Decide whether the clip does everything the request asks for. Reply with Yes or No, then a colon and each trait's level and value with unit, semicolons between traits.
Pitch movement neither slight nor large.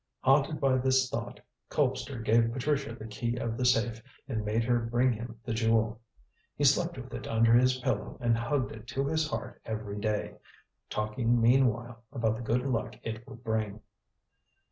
No: narrow, 2.3 semitones